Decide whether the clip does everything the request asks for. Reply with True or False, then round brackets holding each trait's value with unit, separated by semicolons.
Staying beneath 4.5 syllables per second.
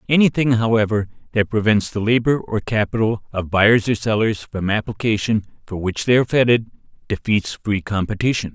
False (5.4 syllables/s)